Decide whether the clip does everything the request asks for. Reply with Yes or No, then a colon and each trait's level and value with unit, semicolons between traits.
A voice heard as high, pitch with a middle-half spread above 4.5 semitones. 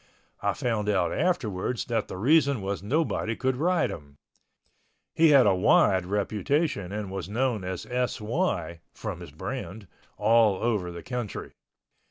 No: low, 105 Hz; average, 5.3 semitones